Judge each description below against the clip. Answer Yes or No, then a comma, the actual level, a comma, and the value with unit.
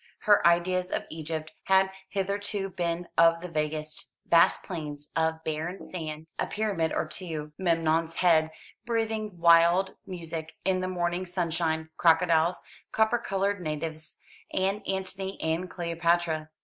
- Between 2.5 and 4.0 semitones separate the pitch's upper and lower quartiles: Yes, average, 2.8 semitones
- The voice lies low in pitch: No, medium, 170 Hz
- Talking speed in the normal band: No, slow, 130 wpm